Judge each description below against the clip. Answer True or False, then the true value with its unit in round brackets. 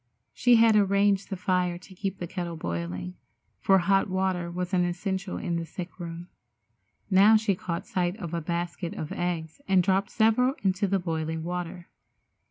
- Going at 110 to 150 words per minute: False (175 wpm)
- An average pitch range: False (2.2 semitones)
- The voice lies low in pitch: False (180 Hz)